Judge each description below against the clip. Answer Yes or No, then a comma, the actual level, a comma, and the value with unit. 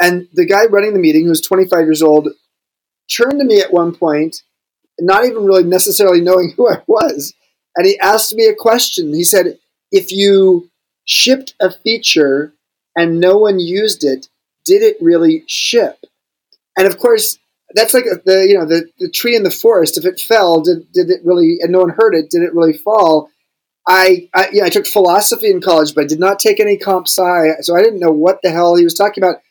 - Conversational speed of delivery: No, fast, 210 wpm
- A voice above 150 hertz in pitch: Yes, high, 190 Hz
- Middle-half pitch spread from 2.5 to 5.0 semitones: No, wide, 5.5 semitones